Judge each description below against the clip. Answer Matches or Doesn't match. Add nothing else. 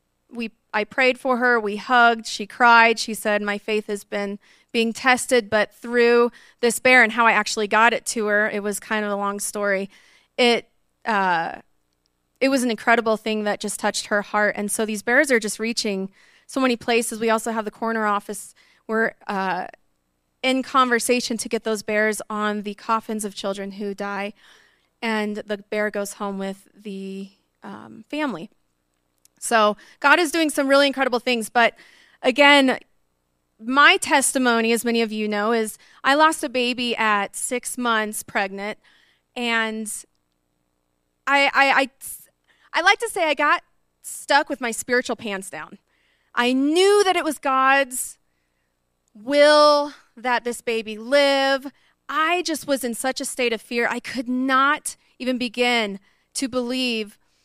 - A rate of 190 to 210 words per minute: Doesn't match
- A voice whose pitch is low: Doesn't match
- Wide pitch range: Doesn't match